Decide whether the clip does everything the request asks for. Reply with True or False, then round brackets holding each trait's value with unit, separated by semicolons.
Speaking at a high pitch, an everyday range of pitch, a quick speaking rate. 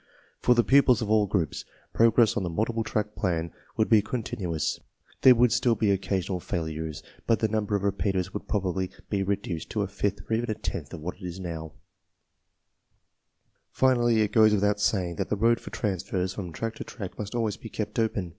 False (105 Hz; 3.3 semitones; 210 wpm)